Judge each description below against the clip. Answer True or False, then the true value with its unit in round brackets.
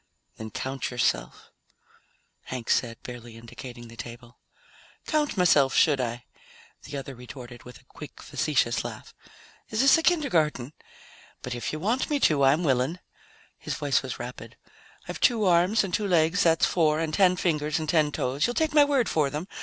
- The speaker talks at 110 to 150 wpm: False (175 wpm)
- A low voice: False (150 Hz)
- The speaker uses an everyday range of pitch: False (6.6 semitones)